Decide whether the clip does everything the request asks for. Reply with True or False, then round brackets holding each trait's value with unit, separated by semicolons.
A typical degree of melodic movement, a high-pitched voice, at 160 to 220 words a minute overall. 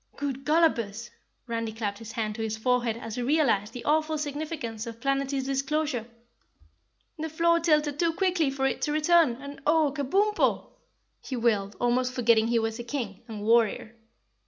True (4.9 semitones; 255 Hz; 165 wpm)